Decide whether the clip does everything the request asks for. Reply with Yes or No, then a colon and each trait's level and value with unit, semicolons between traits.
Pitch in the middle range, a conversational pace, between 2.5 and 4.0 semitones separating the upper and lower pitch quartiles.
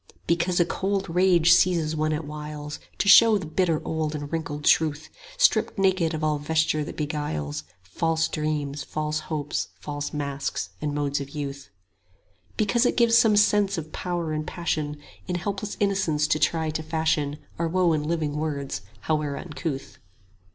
Yes: medium, 155 Hz; average, 165 wpm; average, 2.8 semitones